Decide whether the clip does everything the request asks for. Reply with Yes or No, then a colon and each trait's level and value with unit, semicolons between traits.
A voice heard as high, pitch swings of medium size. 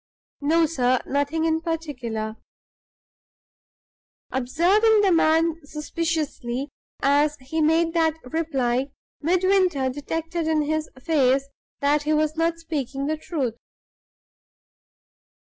Yes: very high, 310 Hz; average, 3.1 semitones